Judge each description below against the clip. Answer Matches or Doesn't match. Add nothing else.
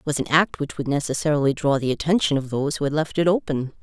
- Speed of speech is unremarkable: Doesn't match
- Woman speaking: Matches